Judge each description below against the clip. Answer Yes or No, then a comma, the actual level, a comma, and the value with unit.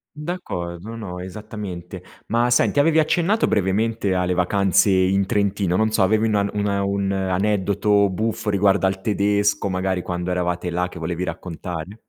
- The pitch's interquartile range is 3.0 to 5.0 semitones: No, narrow, 2.6 semitones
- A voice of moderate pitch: No, low, 100 Hz